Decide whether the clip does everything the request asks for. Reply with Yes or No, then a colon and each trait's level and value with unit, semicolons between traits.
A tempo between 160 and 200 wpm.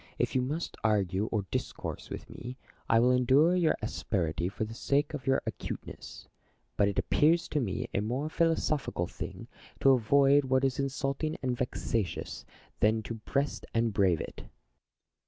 Yes: average, 165 wpm